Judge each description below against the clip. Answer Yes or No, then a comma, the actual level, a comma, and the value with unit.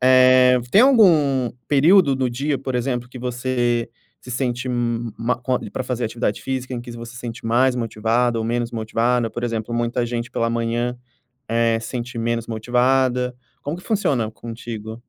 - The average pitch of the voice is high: No, low, 120 Hz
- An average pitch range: No, narrow, 1.7 semitones